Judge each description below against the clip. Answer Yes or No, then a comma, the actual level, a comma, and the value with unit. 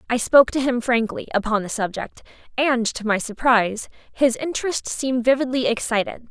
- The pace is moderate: Yes, average, 160 wpm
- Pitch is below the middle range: No, high, 240 Hz